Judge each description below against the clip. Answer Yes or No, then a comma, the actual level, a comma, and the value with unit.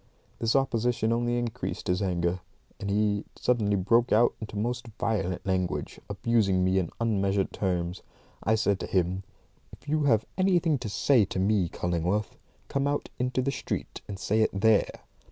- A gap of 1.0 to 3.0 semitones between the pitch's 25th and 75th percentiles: No, average, 4.1 semitones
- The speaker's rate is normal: Yes, average, 165 wpm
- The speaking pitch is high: No, low, 105 Hz